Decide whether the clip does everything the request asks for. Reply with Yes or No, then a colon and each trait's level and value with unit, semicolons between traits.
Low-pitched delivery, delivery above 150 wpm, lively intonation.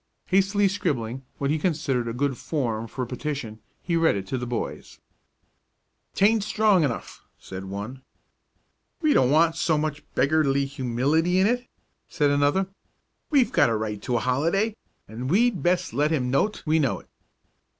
No: medium, 145 Hz; average, 165 wpm; wide, 6.1 semitones